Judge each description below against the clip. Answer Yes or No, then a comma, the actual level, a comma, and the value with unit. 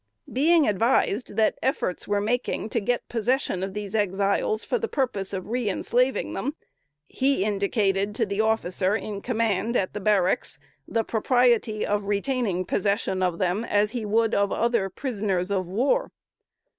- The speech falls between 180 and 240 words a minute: No, average, 155 wpm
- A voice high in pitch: Yes, high, 210 Hz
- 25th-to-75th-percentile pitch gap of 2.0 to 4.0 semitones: Yes, average, 3.4 semitones